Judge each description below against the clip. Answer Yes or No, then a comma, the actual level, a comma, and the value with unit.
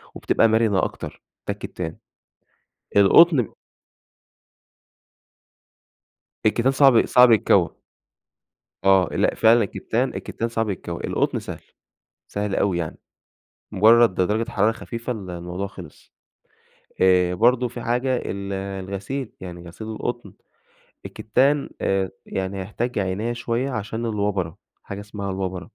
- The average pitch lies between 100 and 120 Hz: Yes, low, 105 Hz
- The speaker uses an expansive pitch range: No, average, 3.7 semitones